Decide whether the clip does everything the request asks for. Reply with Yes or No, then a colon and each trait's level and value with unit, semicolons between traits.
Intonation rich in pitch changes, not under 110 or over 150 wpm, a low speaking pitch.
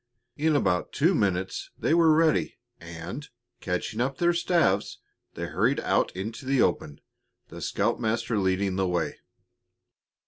Yes: wide, 8.3 semitones; slow, 135 wpm; low, 110 Hz